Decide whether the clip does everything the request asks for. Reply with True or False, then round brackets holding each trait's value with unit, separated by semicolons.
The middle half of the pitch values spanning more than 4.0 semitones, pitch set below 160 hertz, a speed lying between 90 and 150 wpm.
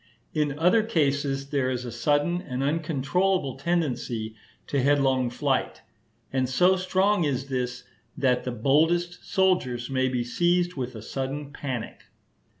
True (5.1 semitones; 140 Hz; 140 wpm)